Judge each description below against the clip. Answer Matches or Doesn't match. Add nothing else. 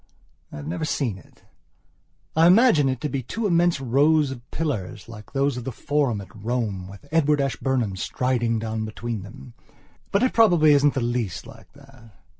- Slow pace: Doesn't match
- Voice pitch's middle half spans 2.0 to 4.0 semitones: Doesn't match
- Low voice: Matches